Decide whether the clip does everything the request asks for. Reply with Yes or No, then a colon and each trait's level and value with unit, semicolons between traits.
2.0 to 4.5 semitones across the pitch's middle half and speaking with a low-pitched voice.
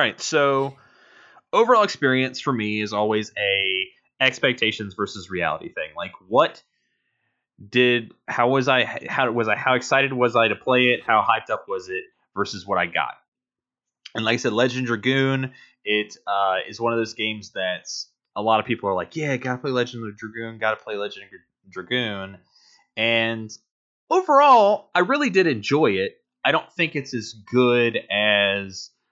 Yes: average, 3.9 semitones; low, 120 Hz